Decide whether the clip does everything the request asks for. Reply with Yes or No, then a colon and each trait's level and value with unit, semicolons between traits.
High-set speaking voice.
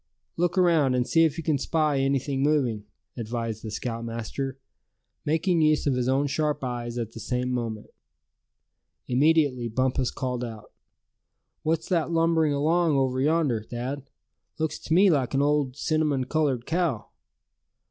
No: low, 135 Hz